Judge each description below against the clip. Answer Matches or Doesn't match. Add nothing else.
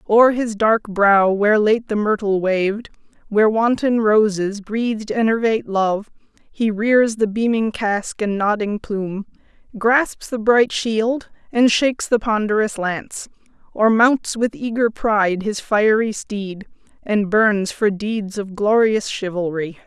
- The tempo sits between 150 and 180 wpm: Doesn't match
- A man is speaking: Doesn't match